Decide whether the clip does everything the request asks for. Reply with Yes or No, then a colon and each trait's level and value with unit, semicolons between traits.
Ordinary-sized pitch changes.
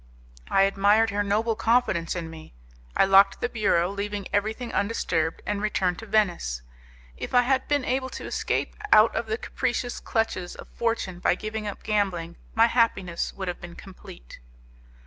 Yes: average, 3.9 semitones